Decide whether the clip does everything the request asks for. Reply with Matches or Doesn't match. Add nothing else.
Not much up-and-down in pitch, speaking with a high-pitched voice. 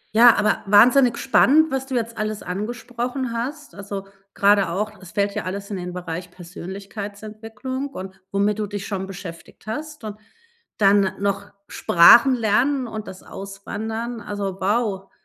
Doesn't match